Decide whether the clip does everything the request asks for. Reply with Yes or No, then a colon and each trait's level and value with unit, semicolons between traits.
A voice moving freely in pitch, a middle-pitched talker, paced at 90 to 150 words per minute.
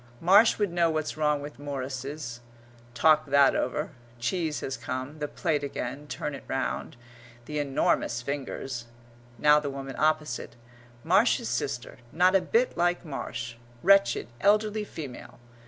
No: average, 3.7 semitones; medium, 150 Hz; average, 140 wpm